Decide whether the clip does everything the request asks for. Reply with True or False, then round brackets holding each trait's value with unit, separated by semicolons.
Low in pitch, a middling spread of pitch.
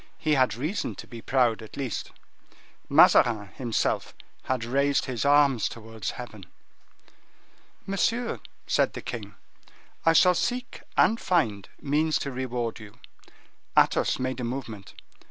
True (130 Hz; 4.4 semitones)